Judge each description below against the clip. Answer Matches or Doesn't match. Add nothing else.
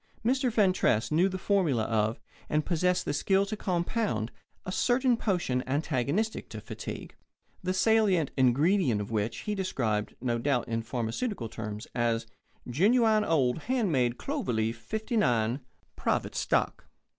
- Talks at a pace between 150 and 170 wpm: Doesn't match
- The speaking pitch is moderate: Matches